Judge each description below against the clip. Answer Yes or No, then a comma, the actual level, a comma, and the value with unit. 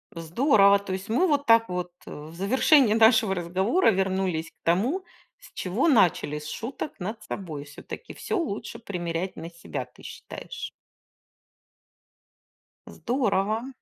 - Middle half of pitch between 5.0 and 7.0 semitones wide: Yes, wide, 5.5 semitones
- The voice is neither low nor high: No, high, 200 Hz